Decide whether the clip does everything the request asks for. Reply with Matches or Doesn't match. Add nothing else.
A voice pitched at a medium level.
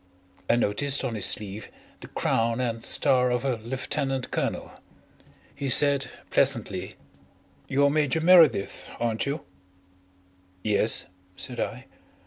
Doesn't match